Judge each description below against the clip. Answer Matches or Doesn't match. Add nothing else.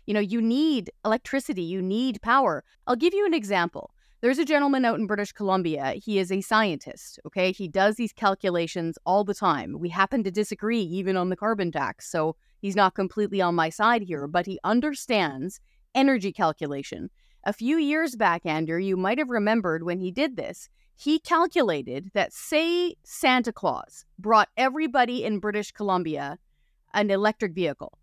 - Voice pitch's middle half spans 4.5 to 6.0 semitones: Matches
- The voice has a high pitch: Matches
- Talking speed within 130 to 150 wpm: Doesn't match